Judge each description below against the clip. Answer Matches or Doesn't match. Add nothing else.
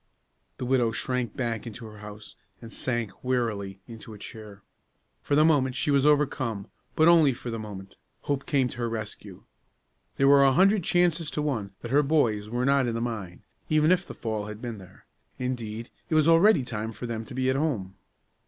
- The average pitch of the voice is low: Matches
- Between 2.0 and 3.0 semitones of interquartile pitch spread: Doesn't match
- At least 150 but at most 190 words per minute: Doesn't match